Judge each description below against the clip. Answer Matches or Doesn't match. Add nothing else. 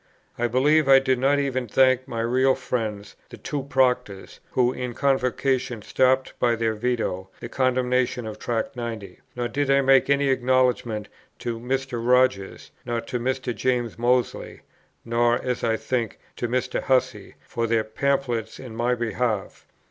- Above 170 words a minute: Doesn't match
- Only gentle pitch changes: Matches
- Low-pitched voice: Matches